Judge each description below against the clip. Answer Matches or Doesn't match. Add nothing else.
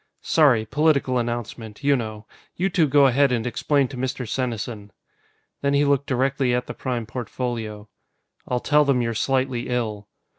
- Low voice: Matches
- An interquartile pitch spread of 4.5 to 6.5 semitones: Doesn't match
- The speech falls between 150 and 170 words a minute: Matches